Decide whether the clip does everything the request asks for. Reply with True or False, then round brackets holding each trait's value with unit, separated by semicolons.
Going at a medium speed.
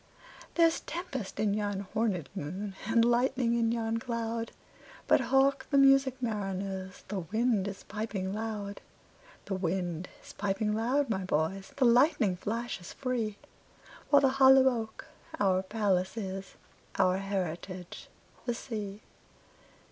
False (110 wpm)